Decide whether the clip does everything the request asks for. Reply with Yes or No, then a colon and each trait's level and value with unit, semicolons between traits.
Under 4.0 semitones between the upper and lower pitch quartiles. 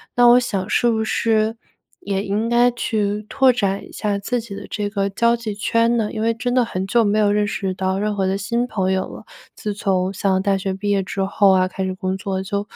Yes: average, 2.9 semitones